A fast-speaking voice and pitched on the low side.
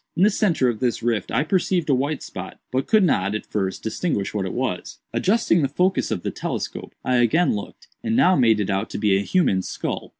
Yes: fast, 230 wpm; low, 130 Hz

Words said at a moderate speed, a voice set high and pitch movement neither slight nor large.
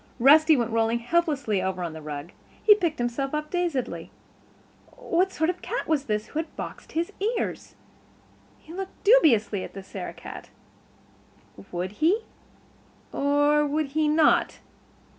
No: average, 150 wpm; very high, 295 Hz; wide, 6.6 semitones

